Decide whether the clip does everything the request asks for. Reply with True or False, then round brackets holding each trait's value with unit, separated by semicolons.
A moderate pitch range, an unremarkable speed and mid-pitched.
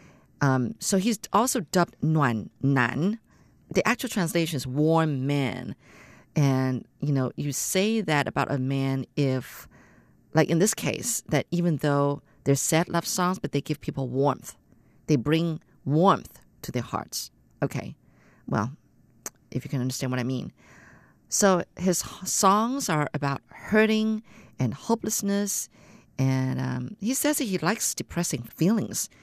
False (6.1 semitones; 145 wpm; 150 Hz)